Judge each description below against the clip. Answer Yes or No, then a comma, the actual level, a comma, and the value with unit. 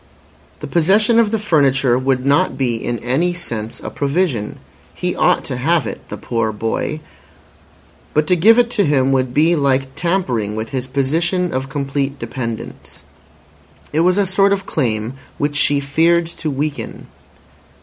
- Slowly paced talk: No, average, 160 wpm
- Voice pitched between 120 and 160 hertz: Yes, medium, 140 Hz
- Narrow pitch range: No, average, 5.1 semitones